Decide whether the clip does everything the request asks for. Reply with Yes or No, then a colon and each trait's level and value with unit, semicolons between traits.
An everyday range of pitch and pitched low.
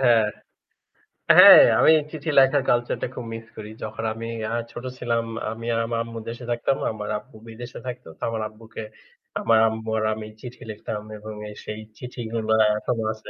No: narrow, 1.7 semitones; low, 115 Hz